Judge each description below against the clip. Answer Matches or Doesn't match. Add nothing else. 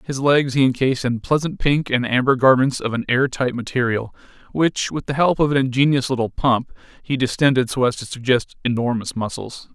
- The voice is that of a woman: Doesn't match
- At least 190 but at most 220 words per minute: Matches